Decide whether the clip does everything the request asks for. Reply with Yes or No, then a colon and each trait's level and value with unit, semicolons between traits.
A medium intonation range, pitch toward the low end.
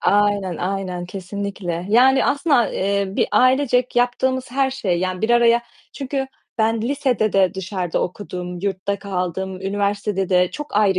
No: average, 4.6 semitones; high, 200 Hz